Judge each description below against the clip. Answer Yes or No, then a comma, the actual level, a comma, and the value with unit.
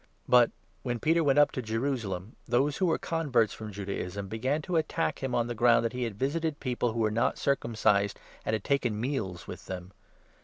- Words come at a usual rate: No, fast, 215 wpm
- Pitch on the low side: Yes, low, 120 Hz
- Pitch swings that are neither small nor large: Yes, average, 4.5 semitones